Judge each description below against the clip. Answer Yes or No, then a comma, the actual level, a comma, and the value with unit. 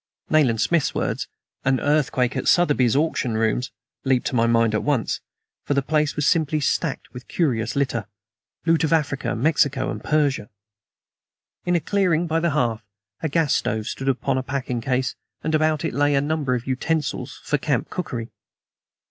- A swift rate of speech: No, average, 175 wpm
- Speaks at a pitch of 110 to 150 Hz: Yes, medium, 140 Hz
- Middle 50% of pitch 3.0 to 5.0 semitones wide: Yes, average, 3.8 semitones